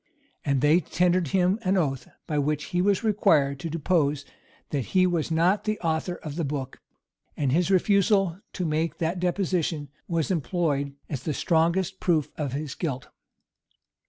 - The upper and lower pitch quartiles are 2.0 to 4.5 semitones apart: Yes, average, 3.8 semitones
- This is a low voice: No, medium, 165 Hz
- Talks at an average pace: Yes, average, 165 wpm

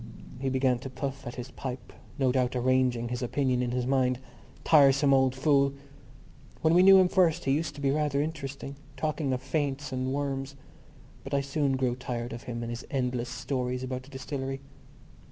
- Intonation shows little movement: Yes, narrow, 1.9 semitones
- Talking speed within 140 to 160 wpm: No, average, 190 wpm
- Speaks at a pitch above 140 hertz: No, low, 135 Hz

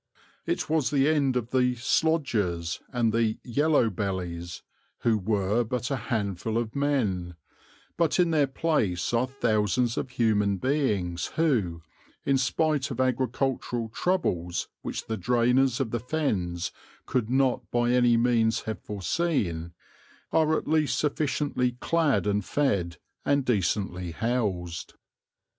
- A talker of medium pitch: No, low, 120 Hz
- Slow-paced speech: Yes, slow, 130 wpm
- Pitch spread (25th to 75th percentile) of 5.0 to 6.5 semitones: Yes, average, 5.3 semitones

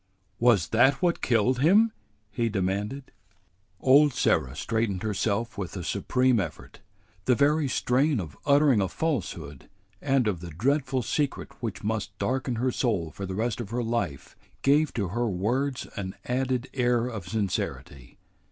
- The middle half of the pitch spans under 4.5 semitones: No, average, 5.0 semitones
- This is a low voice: Yes, low, 120 Hz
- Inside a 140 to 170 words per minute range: Yes, average, 150 wpm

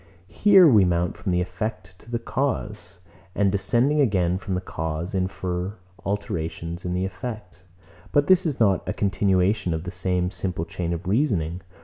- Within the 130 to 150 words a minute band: No, average, 165 wpm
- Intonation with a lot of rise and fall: No, average, 3.3 semitones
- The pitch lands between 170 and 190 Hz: No, very low, 95 Hz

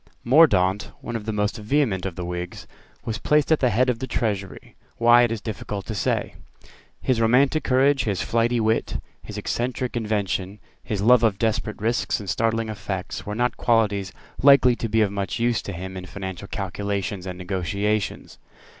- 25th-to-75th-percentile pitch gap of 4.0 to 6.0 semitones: No, average, 3.4 semitones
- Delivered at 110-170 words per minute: No, average, 180 wpm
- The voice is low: Yes, low, 110 Hz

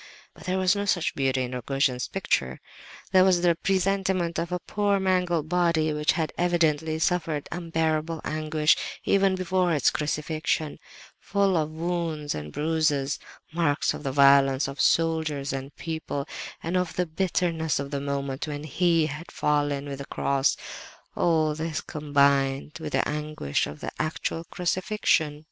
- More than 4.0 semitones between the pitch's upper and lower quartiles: No, average, 3.3 semitones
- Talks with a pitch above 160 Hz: No, medium, 155 Hz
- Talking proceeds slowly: No, average, 150 wpm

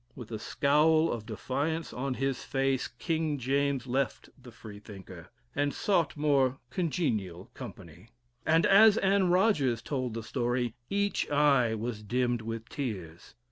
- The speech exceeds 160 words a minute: No, average, 140 wpm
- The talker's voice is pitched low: Yes, low, 130 Hz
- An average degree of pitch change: Yes, average, 4.9 semitones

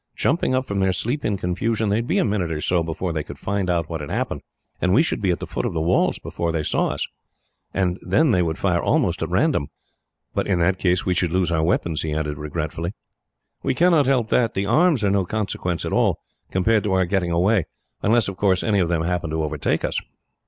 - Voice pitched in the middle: No, very low, 90 Hz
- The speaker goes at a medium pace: No, fast, 245 wpm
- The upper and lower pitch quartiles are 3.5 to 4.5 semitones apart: Yes, average, 4.0 semitones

